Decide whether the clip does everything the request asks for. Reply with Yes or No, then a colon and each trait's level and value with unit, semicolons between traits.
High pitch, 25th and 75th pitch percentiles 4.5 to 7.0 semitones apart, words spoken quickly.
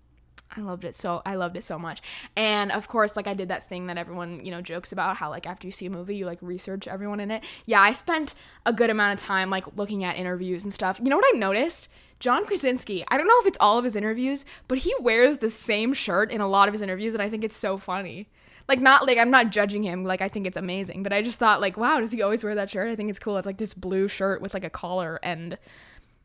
No: high, 200 Hz; average, 3.1 semitones; fast, 280 wpm